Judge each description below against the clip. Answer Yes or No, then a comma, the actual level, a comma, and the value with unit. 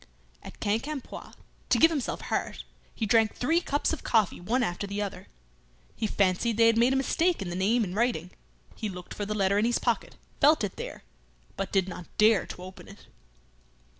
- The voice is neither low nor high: No, high, 220 Hz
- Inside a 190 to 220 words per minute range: Yes, average, 195 wpm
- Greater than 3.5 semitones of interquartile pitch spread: Yes, average, 4.1 semitones